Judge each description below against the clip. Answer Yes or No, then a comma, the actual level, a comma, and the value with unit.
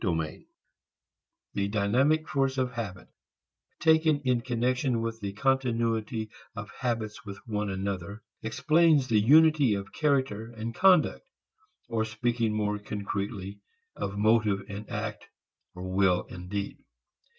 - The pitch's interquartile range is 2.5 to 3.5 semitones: No, average, 4.2 semitones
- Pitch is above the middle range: No, low, 110 Hz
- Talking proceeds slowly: Yes, slow, 120 wpm